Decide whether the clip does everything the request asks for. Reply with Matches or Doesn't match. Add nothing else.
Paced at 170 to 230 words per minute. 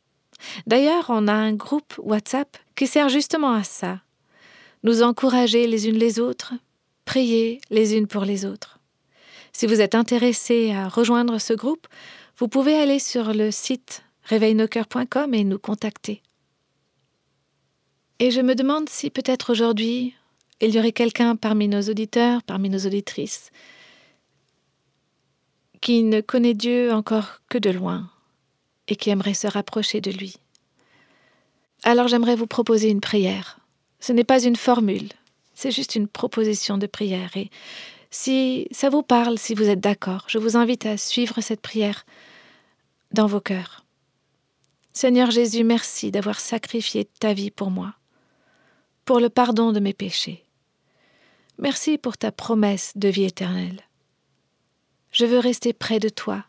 Doesn't match